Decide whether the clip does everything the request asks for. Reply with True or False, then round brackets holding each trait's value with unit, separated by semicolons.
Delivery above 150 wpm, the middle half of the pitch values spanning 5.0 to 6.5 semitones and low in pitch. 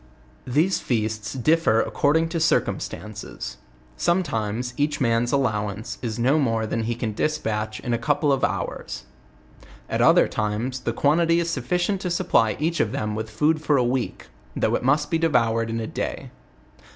True (165 wpm; 5.6 semitones; 125 Hz)